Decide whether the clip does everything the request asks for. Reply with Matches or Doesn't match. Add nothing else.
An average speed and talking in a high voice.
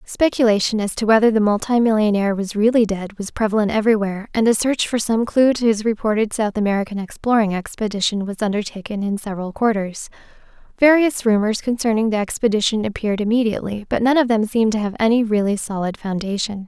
Matches